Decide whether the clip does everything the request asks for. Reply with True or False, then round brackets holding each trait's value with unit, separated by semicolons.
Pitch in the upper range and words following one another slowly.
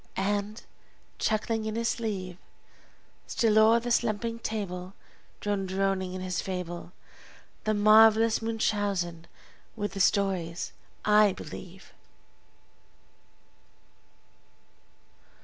True (205 Hz; 90 wpm)